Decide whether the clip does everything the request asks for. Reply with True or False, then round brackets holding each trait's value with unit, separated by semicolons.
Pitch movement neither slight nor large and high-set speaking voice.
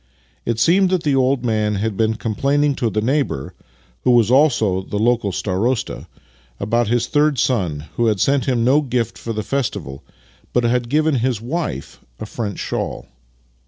False (4.2 semitones; 120 Hz)